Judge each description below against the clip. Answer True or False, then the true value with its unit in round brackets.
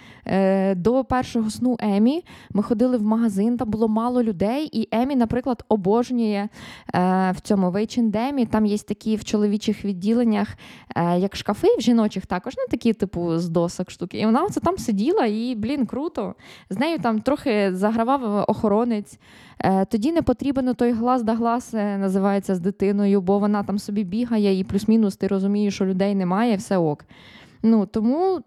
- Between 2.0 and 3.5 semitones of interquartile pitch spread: True (3.2 semitones)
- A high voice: True (215 Hz)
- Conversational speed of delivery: False (165 wpm)